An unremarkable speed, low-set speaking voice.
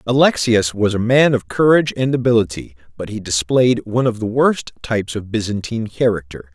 Yes: average, 175 wpm; low, 115 Hz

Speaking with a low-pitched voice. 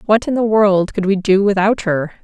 No: high, 200 Hz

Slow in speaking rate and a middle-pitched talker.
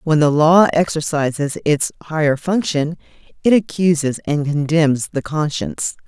Yes: slow, 130 wpm; medium, 155 Hz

